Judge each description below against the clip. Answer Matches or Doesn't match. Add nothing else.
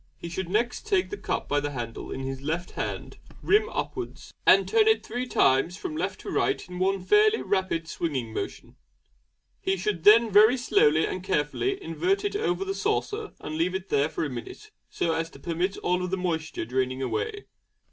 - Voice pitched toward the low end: Doesn't match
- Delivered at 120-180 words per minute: Doesn't match